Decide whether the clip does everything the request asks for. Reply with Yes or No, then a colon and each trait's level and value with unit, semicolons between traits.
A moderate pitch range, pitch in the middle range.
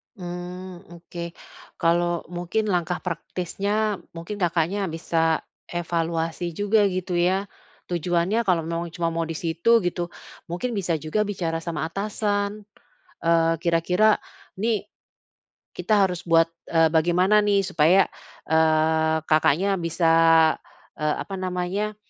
Yes: average, 3.0 semitones; medium, 175 Hz